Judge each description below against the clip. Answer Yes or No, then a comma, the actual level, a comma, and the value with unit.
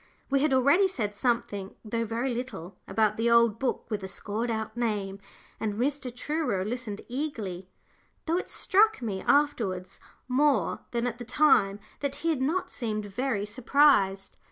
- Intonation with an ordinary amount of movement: Yes, average, 5.0 semitones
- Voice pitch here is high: Yes, high, 235 Hz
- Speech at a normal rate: Yes, average, 160 wpm